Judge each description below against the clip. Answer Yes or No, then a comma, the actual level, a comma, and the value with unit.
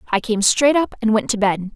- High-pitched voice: Yes, high, 225 Hz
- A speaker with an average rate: No, fast, 275 wpm